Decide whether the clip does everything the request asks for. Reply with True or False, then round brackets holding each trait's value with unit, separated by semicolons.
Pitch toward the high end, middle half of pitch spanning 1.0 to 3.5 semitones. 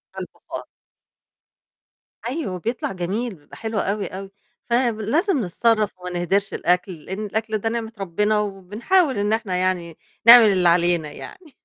False (205 Hz; 4.0 semitones)